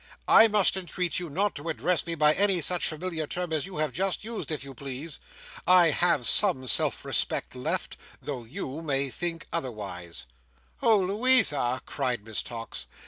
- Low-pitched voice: No, medium, 160 Hz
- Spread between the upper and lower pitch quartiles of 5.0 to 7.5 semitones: Yes, wide, 5.4 semitones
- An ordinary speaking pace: Yes, average, 170 wpm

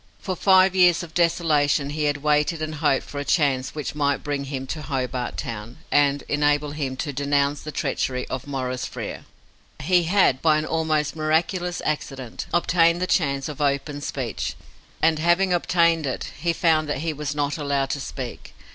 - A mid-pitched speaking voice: Yes, medium, 150 Hz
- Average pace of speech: Yes, average, 180 wpm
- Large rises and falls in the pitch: No, average, 2.8 semitones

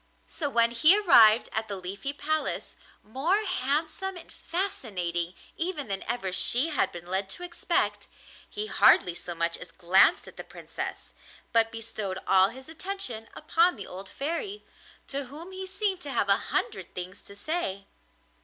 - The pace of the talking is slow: No, average, 165 wpm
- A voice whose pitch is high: Yes, high, 245 Hz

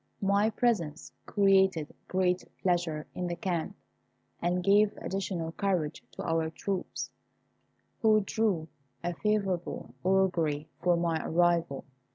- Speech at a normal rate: No, slow, 115 wpm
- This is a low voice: No, medium, 180 Hz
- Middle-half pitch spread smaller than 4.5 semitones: Yes, average, 3.0 semitones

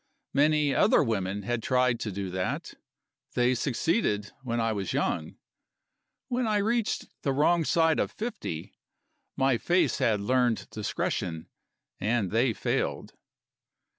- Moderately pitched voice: No, low, 120 Hz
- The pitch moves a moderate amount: No, wide, 6.6 semitones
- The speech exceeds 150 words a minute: No, slow, 135 wpm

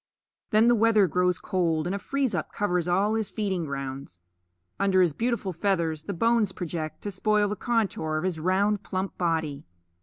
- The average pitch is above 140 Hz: Yes, medium, 185 Hz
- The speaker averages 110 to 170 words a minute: No, average, 180 wpm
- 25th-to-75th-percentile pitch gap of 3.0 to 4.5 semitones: Yes, average, 4.2 semitones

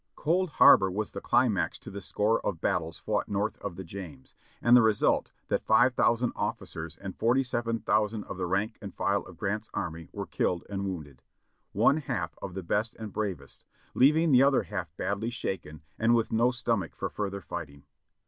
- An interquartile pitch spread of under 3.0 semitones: No, average, 4.3 semitones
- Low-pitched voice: Yes, low, 100 Hz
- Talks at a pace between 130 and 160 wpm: No, average, 190 wpm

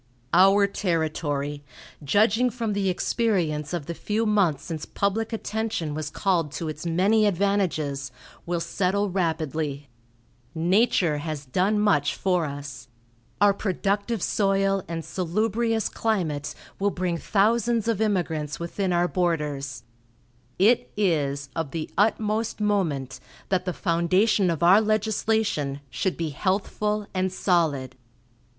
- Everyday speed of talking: No, slow, 125 wpm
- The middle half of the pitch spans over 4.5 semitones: Yes, average, 5.0 semitones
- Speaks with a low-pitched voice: No, medium, 185 Hz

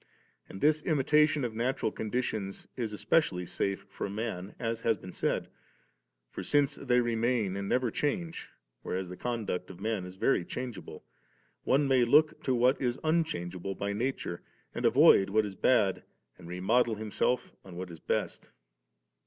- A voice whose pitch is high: No, low, 110 Hz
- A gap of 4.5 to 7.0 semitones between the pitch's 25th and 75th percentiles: Yes, average, 5.0 semitones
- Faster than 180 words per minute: No, average, 165 wpm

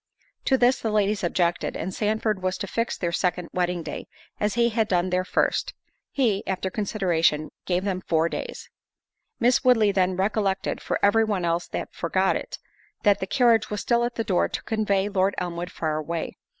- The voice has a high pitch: Yes, high, 195 Hz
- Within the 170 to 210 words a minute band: Yes, average, 190 wpm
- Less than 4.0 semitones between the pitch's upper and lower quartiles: Yes, average, 3.4 semitones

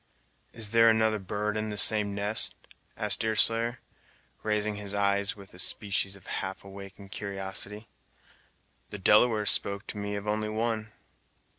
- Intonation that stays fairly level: Yes, narrow, 1.5 semitones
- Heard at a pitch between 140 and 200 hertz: No, low, 105 Hz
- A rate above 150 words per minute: No, average, 145 wpm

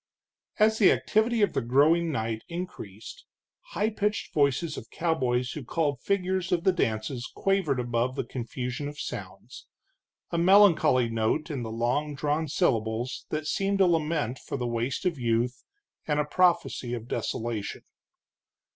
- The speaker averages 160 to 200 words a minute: No, average, 150 wpm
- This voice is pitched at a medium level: Yes, medium, 145 Hz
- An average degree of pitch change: No, wide, 6.3 semitones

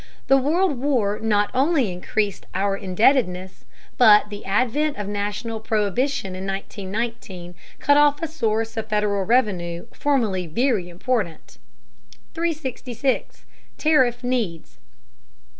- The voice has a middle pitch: No, high, 220 Hz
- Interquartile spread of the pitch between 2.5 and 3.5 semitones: No, average, 4.9 semitones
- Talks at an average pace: No, slow, 110 wpm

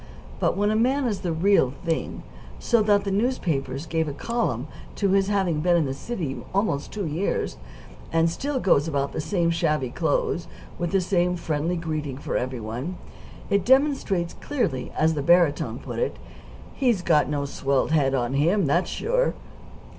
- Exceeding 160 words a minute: Yes, average, 180 wpm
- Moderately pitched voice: Yes, medium, 170 Hz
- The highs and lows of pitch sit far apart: Yes, wide, 5.7 semitones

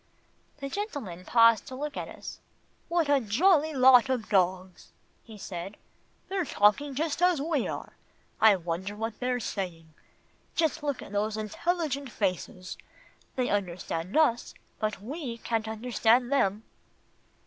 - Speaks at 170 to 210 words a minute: No, slow, 135 wpm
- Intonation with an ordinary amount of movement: No, wide, 5.9 semitones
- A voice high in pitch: Yes, high, 230 Hz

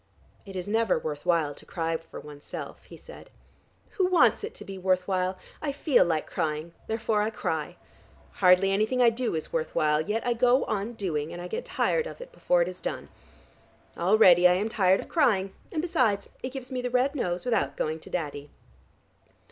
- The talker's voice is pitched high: Yes, high, 195 Hz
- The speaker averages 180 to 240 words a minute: Yes, average, 200 wpm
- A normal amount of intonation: No, wide, 6.7 semitones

